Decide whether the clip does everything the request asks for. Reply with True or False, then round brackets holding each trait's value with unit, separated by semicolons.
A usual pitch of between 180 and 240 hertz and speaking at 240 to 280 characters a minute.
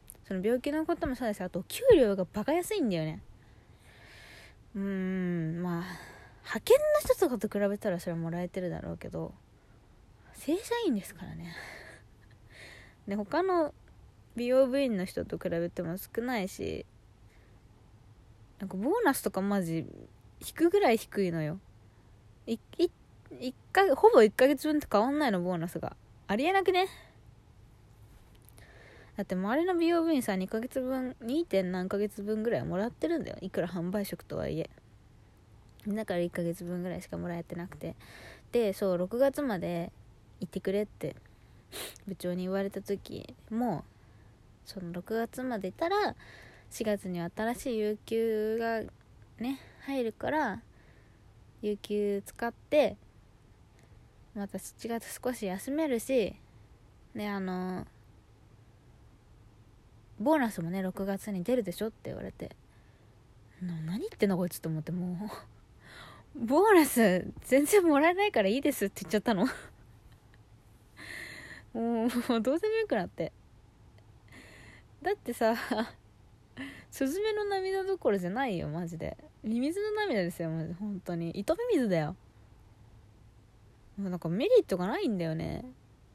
True (185 Hz; 260 characters per minute)